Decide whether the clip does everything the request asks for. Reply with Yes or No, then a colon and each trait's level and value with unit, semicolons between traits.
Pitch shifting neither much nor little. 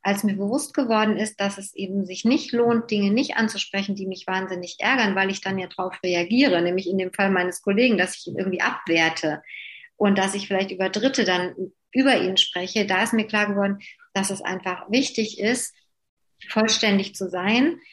Yes: average, 3.1 semitones